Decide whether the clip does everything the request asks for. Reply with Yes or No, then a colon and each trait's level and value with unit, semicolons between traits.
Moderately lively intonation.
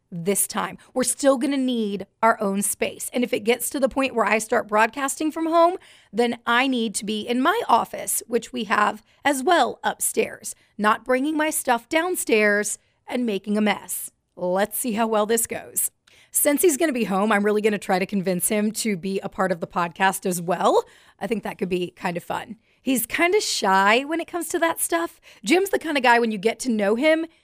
No: wide, 5.8 semitones